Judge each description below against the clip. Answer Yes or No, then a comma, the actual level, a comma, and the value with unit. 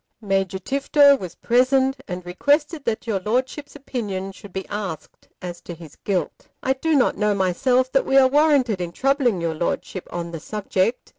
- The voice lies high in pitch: Yes, high, 215 Hz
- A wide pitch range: Yes, wide, 6.5 semitones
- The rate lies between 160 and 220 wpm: Yes, average, 175 wpm